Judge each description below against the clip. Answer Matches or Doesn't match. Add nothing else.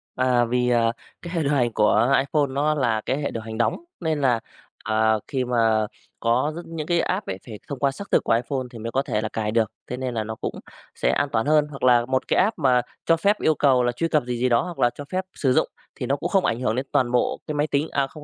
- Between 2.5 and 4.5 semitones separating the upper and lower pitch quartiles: Matches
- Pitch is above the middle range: Doesn't match